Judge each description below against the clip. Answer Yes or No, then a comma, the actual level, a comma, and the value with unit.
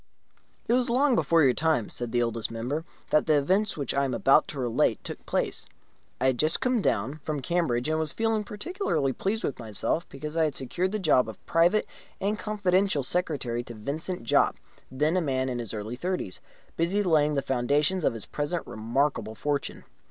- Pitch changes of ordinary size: No, wide, 6.6 semitones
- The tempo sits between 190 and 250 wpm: Yes, average, 195 wpm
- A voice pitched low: No, medium, 150 Hz